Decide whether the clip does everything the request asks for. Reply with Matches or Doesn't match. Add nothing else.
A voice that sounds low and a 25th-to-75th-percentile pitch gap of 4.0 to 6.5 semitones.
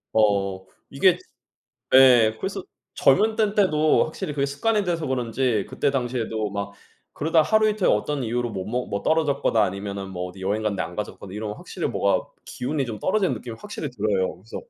Doesn't match